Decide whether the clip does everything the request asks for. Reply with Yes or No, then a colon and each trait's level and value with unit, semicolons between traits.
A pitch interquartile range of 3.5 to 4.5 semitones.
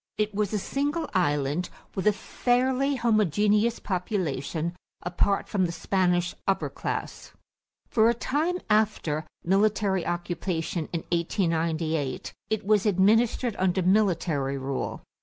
Yes: average, 4.2 semitones